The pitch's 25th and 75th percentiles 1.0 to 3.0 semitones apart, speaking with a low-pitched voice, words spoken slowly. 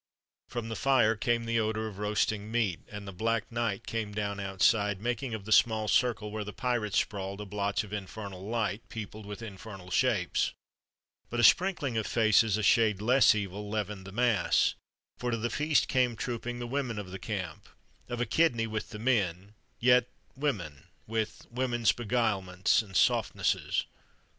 No: average, 2.7 semitones; low, 110 Hz; average, 170 wpm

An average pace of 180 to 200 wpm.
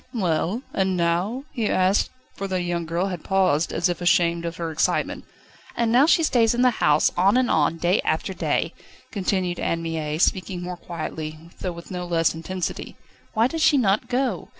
Yes: average, 190 wpm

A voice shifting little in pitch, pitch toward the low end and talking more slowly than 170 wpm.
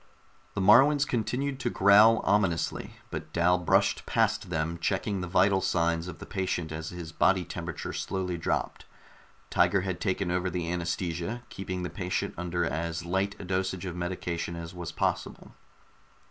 Yes: narrow, 2.3 semitones; very low, 90 Hz; average, 160 wpm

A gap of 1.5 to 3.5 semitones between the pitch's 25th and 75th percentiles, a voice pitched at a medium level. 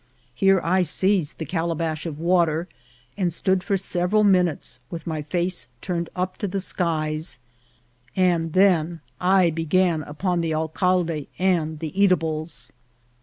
Yes: average, 2.7 semitones; medium, 170 Hz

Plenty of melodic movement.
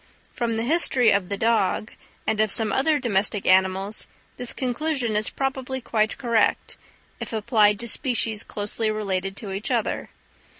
No: average, 3.3 semitones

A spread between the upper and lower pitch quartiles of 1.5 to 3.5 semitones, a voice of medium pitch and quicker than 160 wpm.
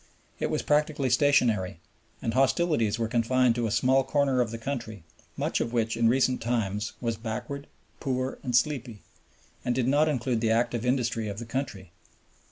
No: average, 2.8 semitones; low, 120 Hz; average, 175 wpm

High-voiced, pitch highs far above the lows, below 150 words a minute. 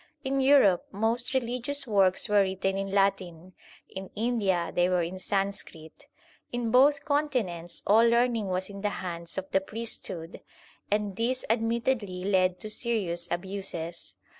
No: high, 200 Hz; average, 4.2 semitones; average, 140 wpm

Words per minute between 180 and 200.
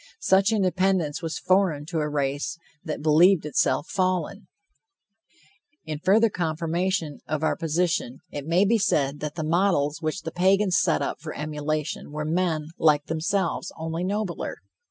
No: average, 150 wpm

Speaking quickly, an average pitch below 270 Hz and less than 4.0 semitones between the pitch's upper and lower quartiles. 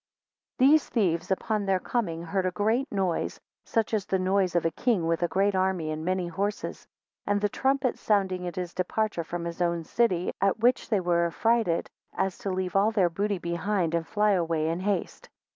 Yes: fast, 210 wpm; high, 190 Hz; average, 3.3 semitones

